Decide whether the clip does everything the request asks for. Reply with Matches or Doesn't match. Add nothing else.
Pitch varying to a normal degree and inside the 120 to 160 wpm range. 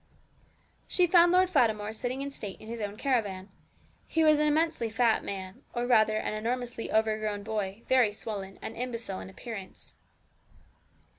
Matches